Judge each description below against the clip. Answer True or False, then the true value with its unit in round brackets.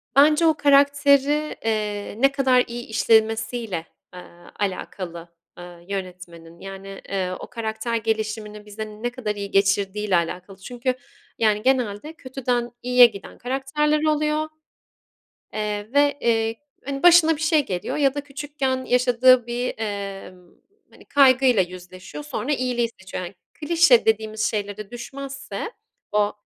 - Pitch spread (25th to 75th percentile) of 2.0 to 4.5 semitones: False (5.2 semitones)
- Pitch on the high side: True (230 Hz)